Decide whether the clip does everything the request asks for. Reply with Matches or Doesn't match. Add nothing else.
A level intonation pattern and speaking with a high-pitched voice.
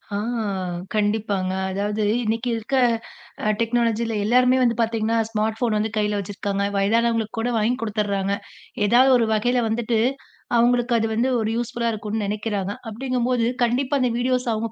Matches